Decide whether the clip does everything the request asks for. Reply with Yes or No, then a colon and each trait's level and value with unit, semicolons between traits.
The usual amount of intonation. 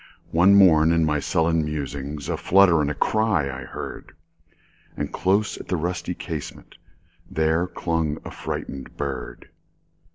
Yes: average, 3.5 semitones